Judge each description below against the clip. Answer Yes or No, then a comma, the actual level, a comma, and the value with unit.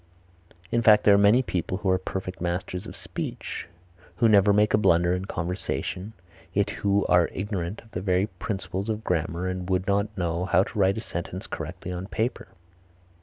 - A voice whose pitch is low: Yes, very low, 95 Hz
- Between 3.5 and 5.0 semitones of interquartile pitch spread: No, narrow, 2.4 semitones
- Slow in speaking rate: No, average, 185 wpm